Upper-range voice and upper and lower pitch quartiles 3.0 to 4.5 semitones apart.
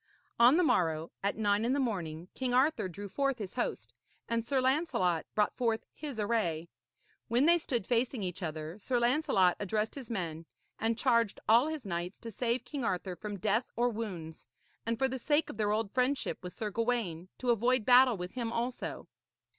No: high, 230 Hz; average, 5.1 semitones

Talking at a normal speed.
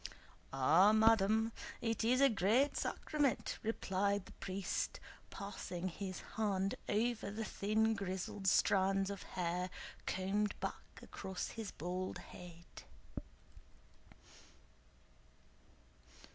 No: slow, 95 wpm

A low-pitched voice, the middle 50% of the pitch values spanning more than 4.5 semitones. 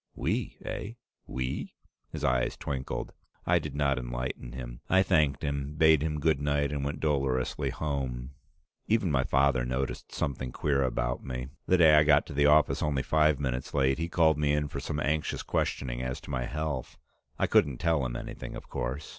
No: very low, 70 Hz; average, 2.9 semitones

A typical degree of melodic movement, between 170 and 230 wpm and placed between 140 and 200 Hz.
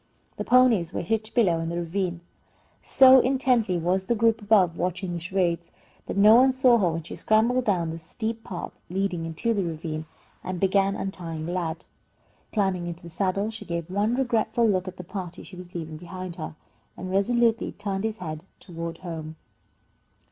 Yes: average, 4.4 semitones; average, 180 wpm; medium, 185 Hz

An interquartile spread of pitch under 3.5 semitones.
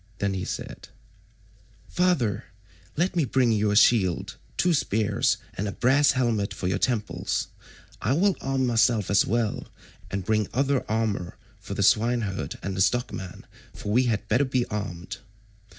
No: average, 4.3 semitones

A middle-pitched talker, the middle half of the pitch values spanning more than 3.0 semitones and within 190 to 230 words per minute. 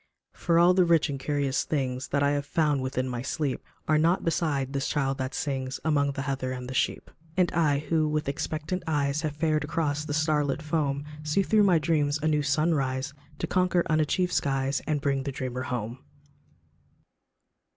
No: medium, 145 Hz; narrow, 2.5 semitones; average, 195 wpm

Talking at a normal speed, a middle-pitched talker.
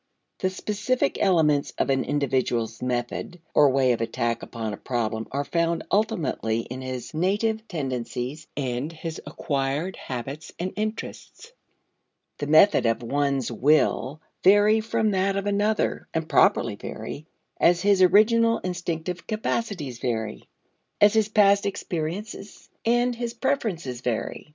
No: slow, 130 wpm; medium, 160 Hz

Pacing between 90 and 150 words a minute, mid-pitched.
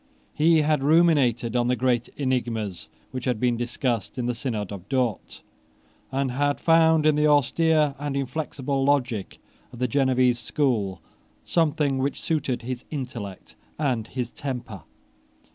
No: average, 145 wpm; low, 130 Hz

